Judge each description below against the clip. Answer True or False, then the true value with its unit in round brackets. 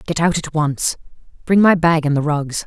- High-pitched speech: False (160 Hz)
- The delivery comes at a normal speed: False (225 wpm)